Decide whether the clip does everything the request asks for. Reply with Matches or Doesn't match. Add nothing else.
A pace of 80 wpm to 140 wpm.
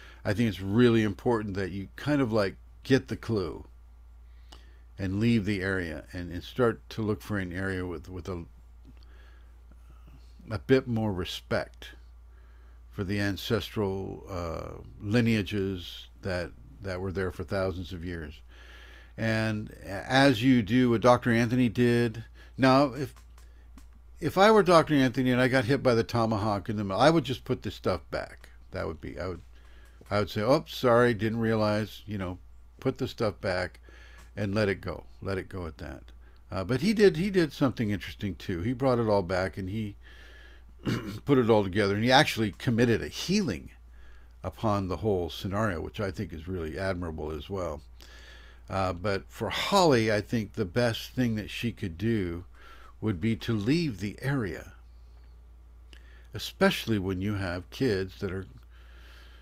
Doesn't match